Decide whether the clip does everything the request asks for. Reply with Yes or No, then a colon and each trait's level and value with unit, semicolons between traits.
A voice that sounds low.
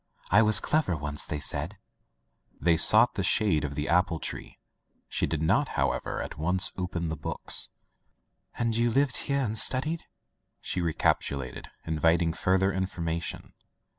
Yes: very low, 90 Hz